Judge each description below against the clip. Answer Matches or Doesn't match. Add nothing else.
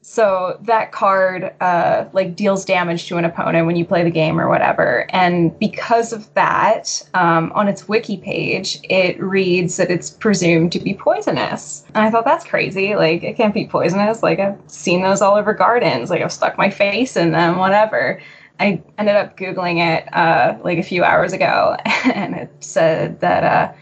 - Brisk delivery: Doesn't match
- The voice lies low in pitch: Doesn't match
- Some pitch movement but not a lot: Matches